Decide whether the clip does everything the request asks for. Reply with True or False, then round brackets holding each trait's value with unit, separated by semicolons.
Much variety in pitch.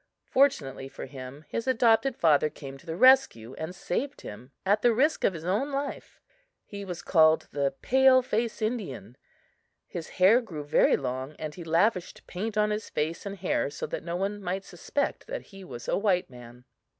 True (7.2 semitones)